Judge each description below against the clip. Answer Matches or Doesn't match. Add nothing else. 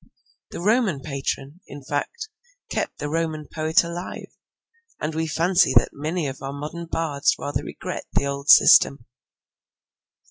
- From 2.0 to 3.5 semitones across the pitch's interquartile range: Matches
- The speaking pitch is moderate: Matches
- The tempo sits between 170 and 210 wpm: Doesn't match